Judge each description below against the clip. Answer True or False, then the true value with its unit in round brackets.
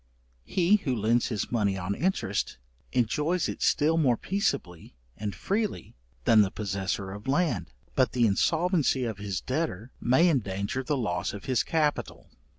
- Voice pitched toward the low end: True (125 Hz)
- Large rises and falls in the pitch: True (7.8 semitones)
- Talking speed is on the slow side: False (155 wpm)